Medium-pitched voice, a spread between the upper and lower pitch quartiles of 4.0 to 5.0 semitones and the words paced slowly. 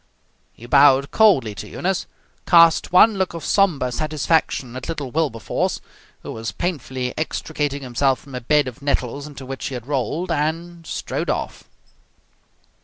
No: medium, 145 Hz; average, 4.3 semitones; average, 150 wpm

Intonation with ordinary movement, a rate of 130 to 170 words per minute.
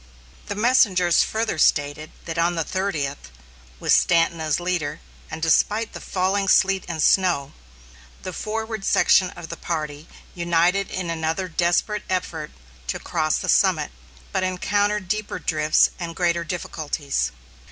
Yes: average, 3.3 semitones; average, 140 wpm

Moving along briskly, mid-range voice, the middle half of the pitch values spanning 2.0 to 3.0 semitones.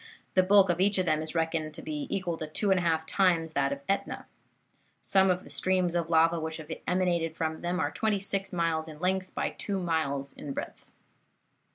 Yes: fast, 215 wpm; medium, 170 Hz; average, 2.7 semitones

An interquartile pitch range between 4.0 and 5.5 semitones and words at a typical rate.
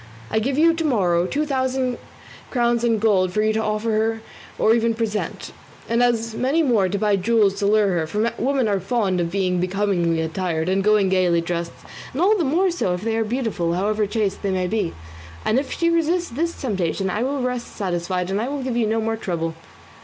No: average, 4.7 semitones; fast, 215 wpm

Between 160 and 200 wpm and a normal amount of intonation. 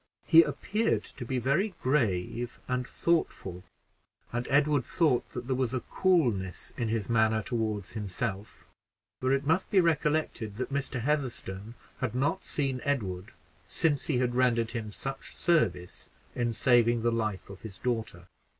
No: average, 150 wpm; average, 4.3 semitones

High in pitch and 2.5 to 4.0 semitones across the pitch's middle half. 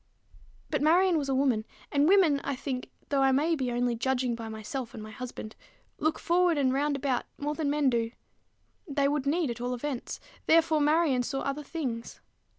Yes: very high, 275 Hz; average, 3.4 semitones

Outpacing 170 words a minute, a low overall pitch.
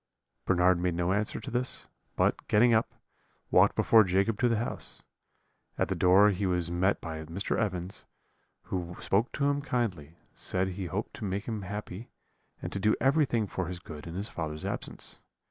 Yes: average, 180 wpm; very low, 95 Hz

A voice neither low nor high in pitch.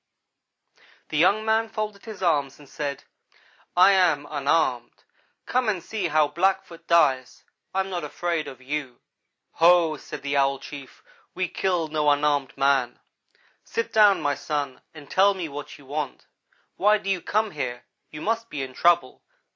Yes: medium, 155 Hz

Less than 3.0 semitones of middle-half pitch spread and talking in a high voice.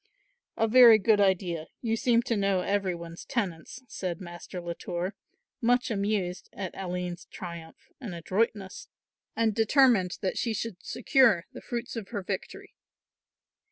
No: average, 4.2 semitones; high, 195 Hz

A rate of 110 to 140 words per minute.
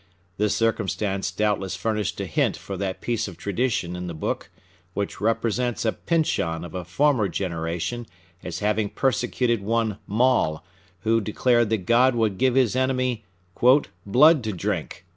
No: average, 150 wpm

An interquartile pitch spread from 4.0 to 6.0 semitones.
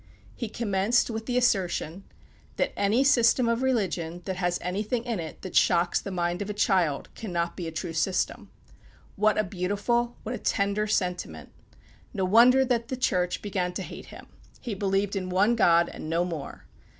Yes: average, 4.4 semitones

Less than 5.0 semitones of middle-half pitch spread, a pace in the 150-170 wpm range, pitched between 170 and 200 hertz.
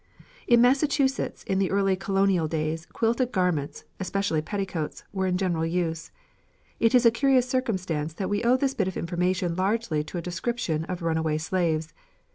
No: wide, 5.6 semitones; average, 165 wpm; medium, 185 Hz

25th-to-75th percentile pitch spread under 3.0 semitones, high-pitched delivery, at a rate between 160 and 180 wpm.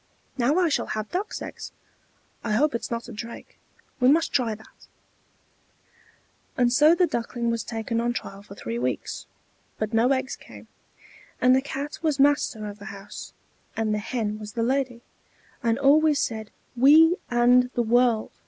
No: average, 3.9 semitones; high, 240 Hz; average, 170 wpm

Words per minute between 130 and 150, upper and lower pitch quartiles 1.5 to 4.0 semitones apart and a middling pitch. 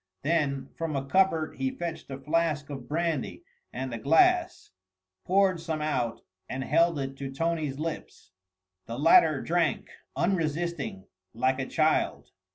Yes: average, 140 wpm; average, 3.7 semitones; medium, 155 Hz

